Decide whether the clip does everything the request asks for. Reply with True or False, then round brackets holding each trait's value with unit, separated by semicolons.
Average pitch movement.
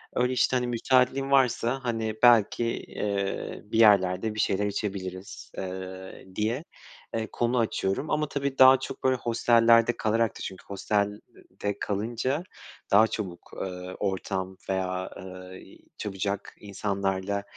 True (3.8 semitones)